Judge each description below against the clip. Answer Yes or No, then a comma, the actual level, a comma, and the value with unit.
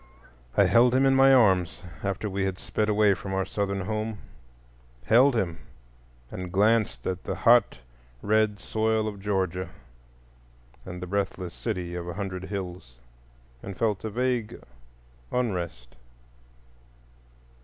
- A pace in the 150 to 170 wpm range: No, slow, 135 wpm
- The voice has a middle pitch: No, low, 100 Hz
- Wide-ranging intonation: No, average, 3.4 semitones